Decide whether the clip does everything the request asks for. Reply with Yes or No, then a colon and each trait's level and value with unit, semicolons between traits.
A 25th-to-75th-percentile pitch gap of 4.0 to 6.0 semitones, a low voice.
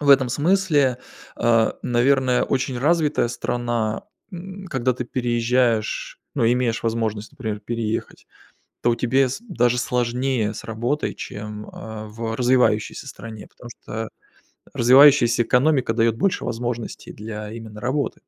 No: average, 2.7 semitones; low, 120 Hz